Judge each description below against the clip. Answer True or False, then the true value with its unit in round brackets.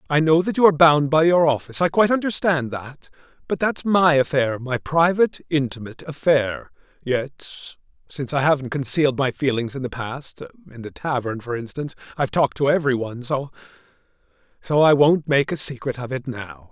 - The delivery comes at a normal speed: True (185 wpm)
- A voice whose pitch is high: False (140 Hz)